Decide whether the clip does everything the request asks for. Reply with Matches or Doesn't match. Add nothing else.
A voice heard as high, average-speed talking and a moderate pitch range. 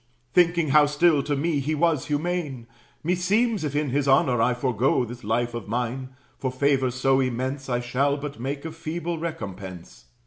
Doesn't match